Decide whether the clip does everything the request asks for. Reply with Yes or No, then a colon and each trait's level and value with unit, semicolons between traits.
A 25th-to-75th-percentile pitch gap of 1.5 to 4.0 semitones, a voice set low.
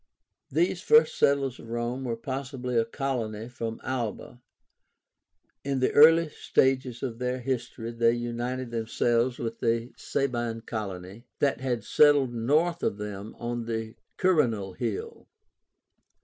Yes: average, 2.7 semitones; low, 120 Hz